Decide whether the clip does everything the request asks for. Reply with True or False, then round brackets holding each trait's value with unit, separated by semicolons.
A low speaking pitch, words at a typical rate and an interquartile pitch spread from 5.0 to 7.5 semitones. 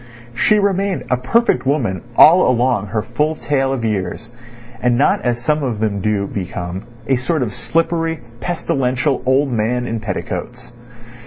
True (125 Hz; 150 wpm; 5.4 semitones)